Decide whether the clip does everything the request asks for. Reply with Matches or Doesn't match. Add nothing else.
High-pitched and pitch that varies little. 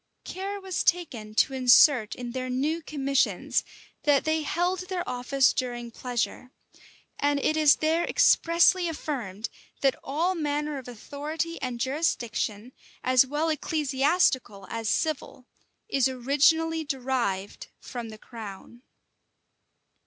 Doesn't match